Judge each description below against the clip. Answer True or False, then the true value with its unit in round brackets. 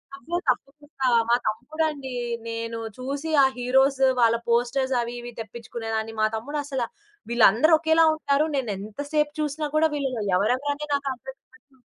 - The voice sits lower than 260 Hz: False (265 Hz)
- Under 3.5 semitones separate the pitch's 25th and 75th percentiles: False (3.8 semitones)